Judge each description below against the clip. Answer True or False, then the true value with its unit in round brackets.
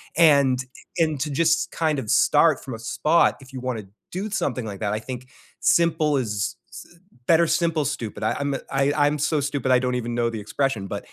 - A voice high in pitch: False (135 Hz)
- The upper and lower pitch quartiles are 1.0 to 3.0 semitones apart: False (4.4 semitones)